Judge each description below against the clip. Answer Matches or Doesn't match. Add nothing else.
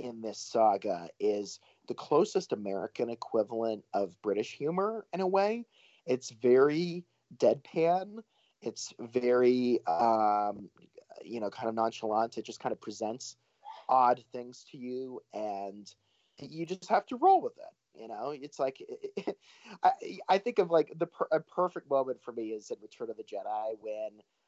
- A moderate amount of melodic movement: Doesn't match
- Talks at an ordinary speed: Matches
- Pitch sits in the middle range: Doesn't match